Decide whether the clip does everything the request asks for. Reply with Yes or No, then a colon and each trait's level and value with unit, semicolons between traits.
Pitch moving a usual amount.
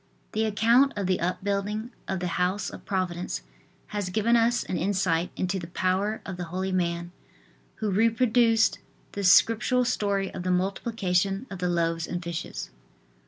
Yes: average, 3.3 semitones